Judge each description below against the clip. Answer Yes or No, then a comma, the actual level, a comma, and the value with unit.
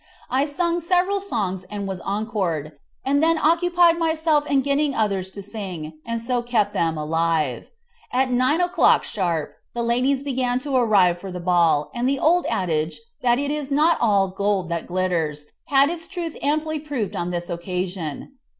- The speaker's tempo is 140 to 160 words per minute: No, average, 170 wpm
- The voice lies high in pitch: Yes, high, 235 Hz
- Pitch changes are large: Yes, wide, 8.3 semitones